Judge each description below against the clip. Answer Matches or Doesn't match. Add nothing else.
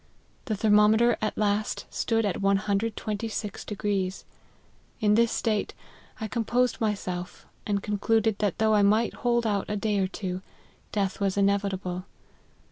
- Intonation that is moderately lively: Doesn't match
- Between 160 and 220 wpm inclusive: Doesn't match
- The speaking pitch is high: Matches